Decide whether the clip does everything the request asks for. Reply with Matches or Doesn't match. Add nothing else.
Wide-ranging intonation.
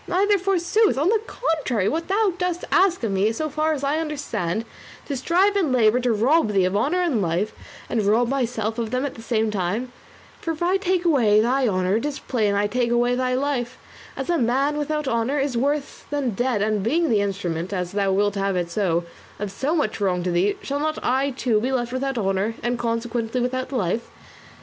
Matches